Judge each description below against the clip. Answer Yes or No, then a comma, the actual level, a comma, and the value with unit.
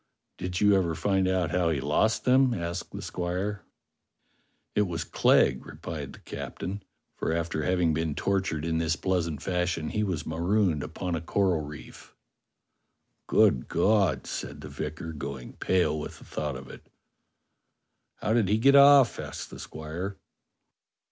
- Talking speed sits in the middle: Yes, average, 155 wpm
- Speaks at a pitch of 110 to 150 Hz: No, very low, 90 Hz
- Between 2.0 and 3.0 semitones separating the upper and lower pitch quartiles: No, average, 3.7 semitones